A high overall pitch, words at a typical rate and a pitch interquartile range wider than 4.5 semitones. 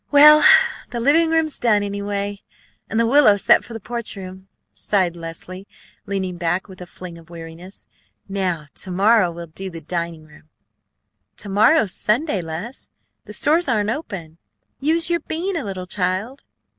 Yes: high, 200 Hz; average, 160 wpm; average, 5.2 semitones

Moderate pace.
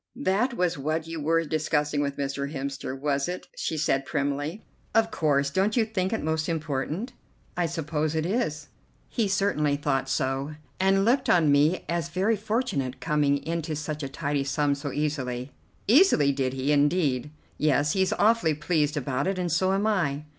Yes: average, 175 wpm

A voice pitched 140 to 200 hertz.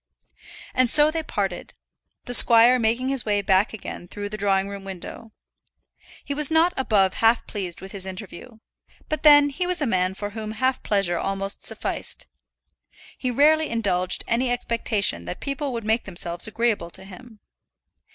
No: high, 220 Hz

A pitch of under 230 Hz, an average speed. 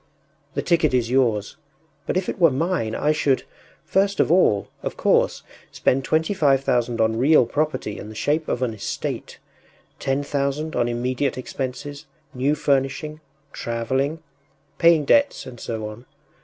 Yes: low, 135 Hz; average, 155 wpm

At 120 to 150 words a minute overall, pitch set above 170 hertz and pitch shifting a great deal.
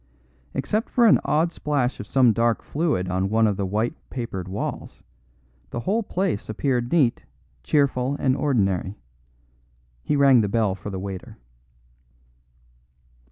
No: average, 140 wpm; low, 120 Hz; wide, 6.2 semitones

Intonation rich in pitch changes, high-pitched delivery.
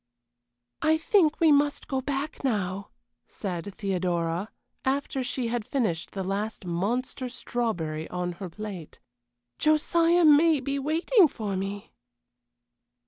Yes: wide, 7.4 semitones; high, 235 Hz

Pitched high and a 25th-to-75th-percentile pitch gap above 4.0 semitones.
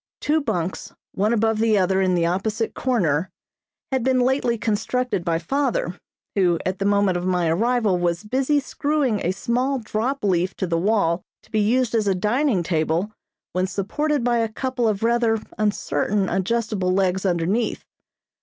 Yes: high, 210 Hz; average, 4.6 semitones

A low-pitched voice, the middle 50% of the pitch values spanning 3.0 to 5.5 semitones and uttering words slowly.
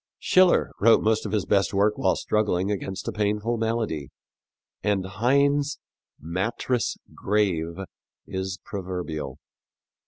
Yes: low, 105 Hz; average, 3.3 semitones; slow, 115 wpm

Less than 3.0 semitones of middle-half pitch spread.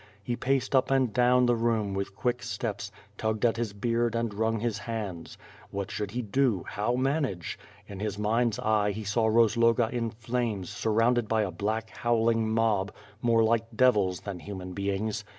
Yes: narrow, 2.5 semitones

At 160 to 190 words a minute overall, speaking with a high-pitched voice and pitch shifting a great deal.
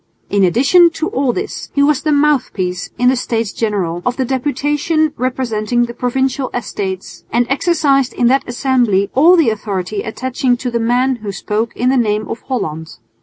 No: average, 175 wpm; high, 245 Hz; average, 4.1 semitones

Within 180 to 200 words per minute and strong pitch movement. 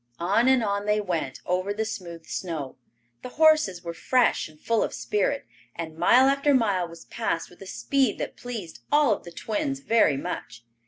Yes: average, 190 wpm; wide, 6.9 semitones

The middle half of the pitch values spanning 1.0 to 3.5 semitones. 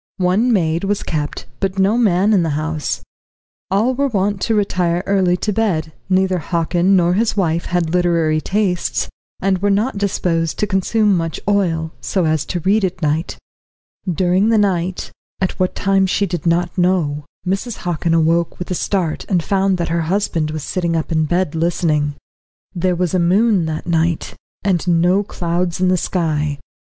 Yes: average, 2.8 semitones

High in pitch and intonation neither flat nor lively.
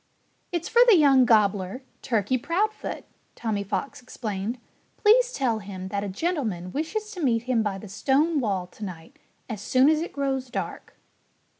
No: high, 245 Hz; wide, 7.1 semitones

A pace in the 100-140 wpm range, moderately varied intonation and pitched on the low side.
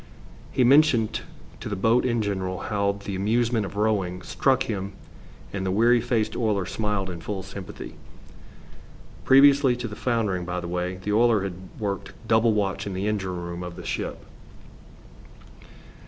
No: average, 160 wpm; average, 3.5 semitones; low, 105 Hz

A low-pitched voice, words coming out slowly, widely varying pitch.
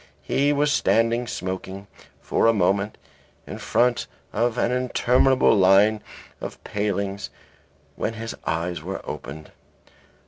No: low, 105 Hz; slow, 125 wpm; average, 4.0 semitones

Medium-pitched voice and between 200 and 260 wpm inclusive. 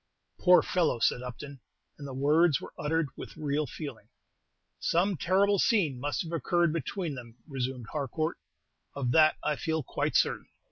No: medium, 150 Hz; average, 155 wpm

